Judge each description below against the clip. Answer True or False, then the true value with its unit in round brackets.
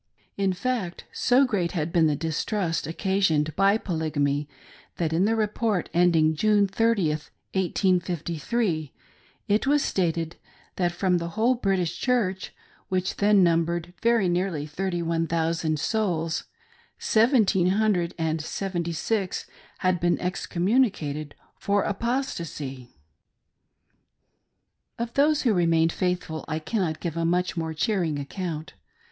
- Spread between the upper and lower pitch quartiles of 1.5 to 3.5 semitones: False (3.9 semitones)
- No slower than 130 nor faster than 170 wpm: True (135 wpm)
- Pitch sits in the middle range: True (180 Hz)